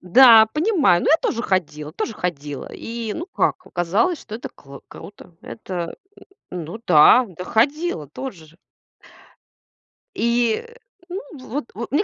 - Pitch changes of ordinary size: No, wide, 7.1 semitones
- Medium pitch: No, high, 220 Hz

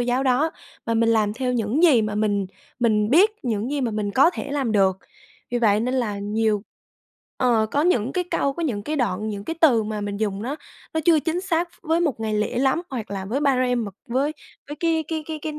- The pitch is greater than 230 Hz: Yes, high, 245 Hz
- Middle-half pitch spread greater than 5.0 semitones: Yes, wide, 5.6 semitones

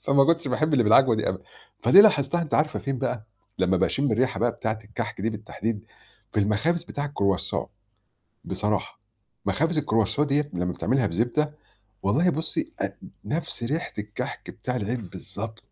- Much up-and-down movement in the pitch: Yes, wide, 5.8 semitones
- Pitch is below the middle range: Yes, low, 120 Hz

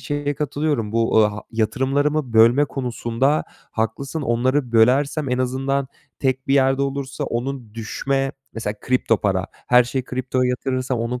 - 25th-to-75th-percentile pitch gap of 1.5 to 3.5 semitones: Yes, average, 3.0 semitones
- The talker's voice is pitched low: Yes, low, 130 Hz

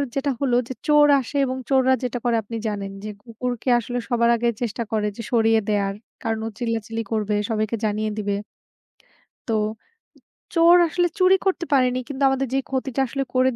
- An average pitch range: Yes, average, 3.3 semitones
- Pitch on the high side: Yes, high, 240 Hz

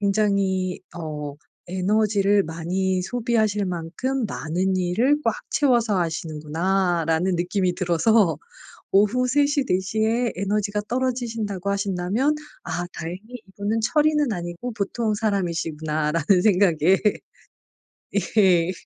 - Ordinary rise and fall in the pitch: Yes, average, 4.1 semitones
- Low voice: No, high, 195 Hz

